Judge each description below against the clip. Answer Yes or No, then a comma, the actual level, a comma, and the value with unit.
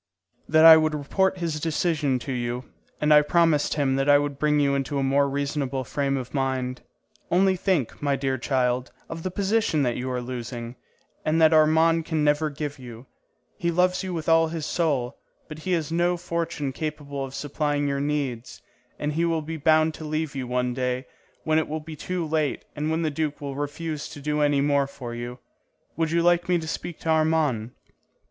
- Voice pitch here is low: No, medium, 150 Hz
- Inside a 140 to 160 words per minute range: No, fast, 205 wpm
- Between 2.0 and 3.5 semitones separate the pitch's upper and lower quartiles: Yes, average, 3.0 semitones